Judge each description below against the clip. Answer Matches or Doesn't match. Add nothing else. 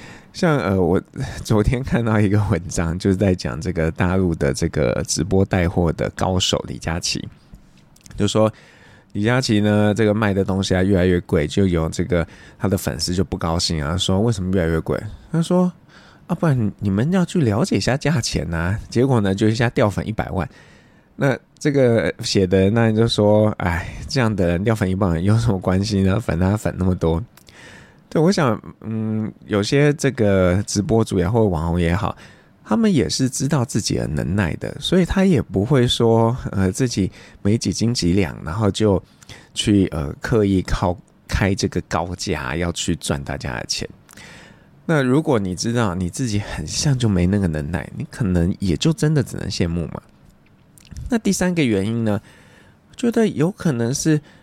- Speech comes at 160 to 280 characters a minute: Matches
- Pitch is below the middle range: Matches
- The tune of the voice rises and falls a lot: Doesn't match